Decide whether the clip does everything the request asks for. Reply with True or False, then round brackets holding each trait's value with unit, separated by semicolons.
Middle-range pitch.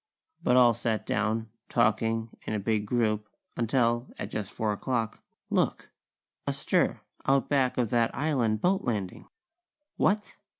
False (115 Hz)